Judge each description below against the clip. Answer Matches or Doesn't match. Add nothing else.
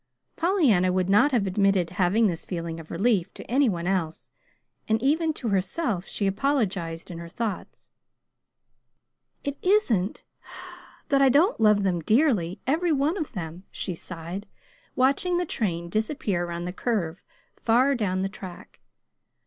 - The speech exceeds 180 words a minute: Doesn't match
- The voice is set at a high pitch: Matches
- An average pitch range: Doesn't match